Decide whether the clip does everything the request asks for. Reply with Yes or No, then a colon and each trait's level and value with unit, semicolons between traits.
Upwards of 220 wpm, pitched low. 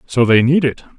Yes: fast, 245 wpm; low, 130 Hz